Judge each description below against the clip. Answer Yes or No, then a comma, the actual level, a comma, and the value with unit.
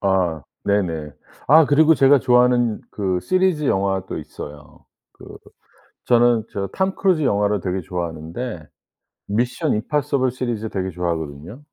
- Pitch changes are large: Yes, wide, 6.2 semitones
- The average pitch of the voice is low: Yes, low, 105 Hz